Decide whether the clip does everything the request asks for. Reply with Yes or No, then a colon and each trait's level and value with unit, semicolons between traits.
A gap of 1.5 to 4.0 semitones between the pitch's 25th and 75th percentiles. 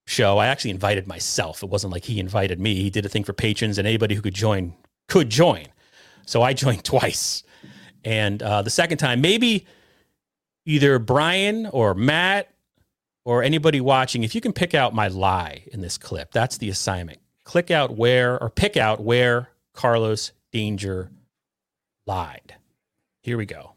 No: average, 4.6 semitones